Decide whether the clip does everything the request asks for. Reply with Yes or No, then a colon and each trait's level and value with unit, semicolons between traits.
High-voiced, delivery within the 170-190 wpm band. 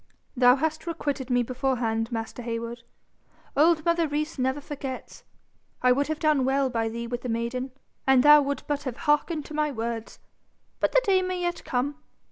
Yes: very high, 270 Hz; average, 180 wpm